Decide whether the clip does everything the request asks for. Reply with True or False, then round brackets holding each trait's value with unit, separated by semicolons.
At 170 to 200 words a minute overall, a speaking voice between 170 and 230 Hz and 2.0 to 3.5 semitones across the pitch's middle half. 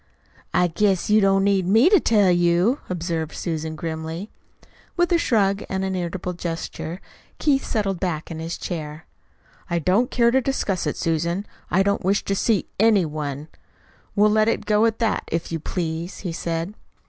False (175 wpm; 185 Hz; 4.1 semitones)